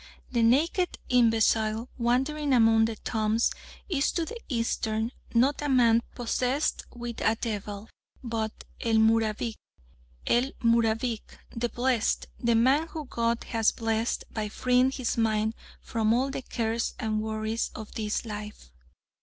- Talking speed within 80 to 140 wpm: Yes, slow, 135 wpm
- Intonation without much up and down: Yes, narrow, 2.2 semitones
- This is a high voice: Yes, high, 230 Hz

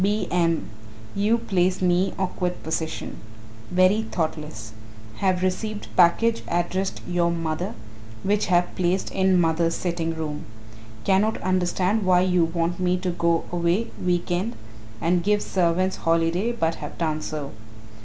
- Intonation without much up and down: Yes, narrow, 2.2 semitones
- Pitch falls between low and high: Yes, medium, 180 Hz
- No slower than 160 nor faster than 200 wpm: No, slow, 135 wpm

